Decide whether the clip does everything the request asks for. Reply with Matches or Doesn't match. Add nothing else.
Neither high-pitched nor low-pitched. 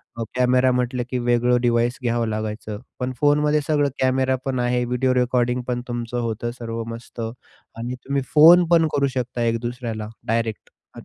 Doesn't match